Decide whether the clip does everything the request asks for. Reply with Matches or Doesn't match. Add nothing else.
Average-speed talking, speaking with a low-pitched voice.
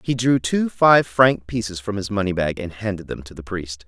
Doesn't match